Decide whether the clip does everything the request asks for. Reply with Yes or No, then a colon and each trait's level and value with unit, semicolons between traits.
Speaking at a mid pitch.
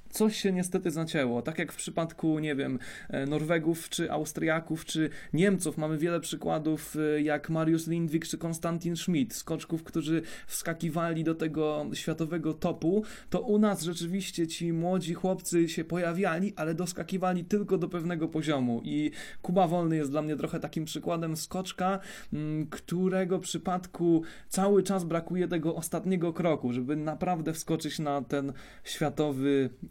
Yes: medium, 165 Hz